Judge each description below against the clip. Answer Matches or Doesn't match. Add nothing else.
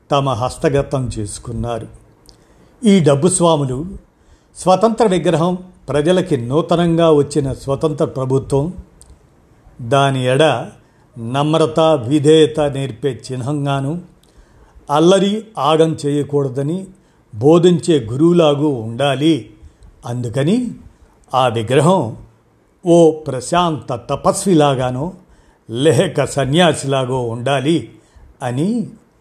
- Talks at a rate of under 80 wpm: Matches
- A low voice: Doesn't match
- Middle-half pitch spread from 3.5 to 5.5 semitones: Matches